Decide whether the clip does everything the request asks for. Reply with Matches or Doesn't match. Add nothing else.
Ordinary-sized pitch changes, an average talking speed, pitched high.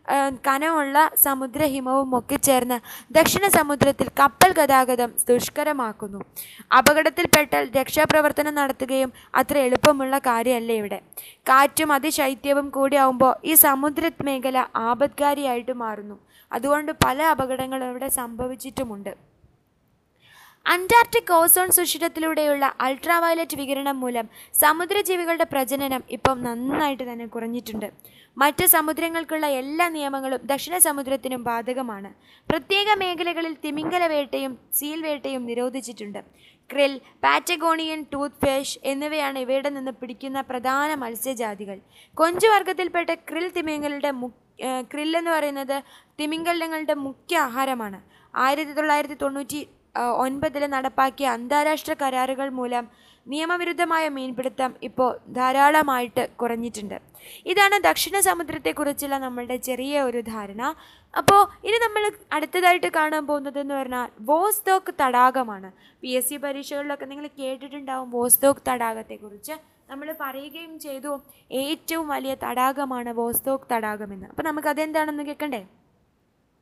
Matches